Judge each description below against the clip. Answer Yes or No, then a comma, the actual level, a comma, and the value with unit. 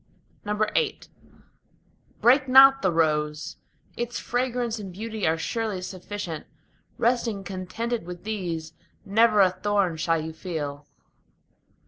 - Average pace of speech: No, slow, 110 wpm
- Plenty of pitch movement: Yes, wide, 5.7 semitones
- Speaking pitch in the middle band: No, high, 200 Hz